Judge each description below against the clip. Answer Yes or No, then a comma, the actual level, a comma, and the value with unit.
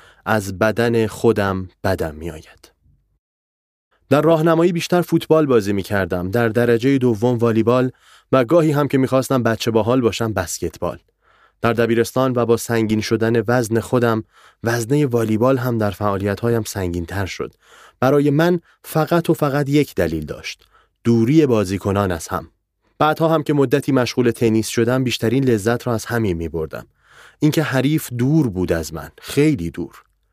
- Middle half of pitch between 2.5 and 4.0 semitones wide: No, average, 5.0 semitones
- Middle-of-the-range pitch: No, low, 115 Hz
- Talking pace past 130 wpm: Yes, fast, 155 wpm